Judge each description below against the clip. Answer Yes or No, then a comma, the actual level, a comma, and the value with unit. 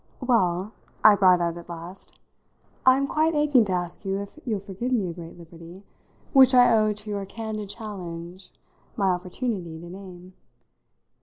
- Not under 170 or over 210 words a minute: No, average, 160 wpm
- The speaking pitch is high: Yes, high, 195 Hz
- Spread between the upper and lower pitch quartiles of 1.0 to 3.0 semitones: No, average, 4.2 semitones